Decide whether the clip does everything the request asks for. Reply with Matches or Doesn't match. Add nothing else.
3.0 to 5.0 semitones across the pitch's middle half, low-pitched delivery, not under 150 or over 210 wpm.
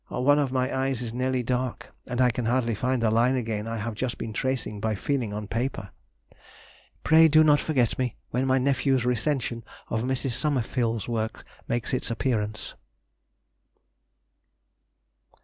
Doesn't match